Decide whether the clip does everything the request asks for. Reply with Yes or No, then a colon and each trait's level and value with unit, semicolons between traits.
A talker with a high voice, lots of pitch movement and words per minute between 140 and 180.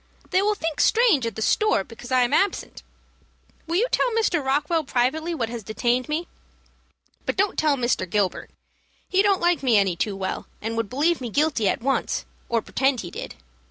No: very high, 265 Hz; wide, 6.9 semitones; average, 195 wpm